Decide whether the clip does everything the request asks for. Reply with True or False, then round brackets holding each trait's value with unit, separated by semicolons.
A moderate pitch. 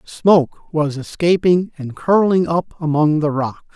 True (160 Hz)